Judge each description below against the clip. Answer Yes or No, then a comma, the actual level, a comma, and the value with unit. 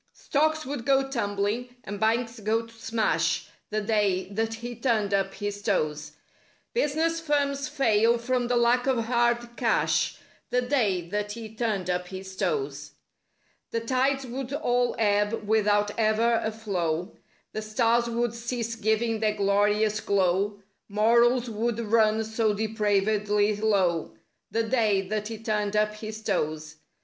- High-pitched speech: Yes, high, 220 Hz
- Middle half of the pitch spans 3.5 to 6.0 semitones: No, narrow, 2.5 semitones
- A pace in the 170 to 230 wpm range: No, average, 145 wpm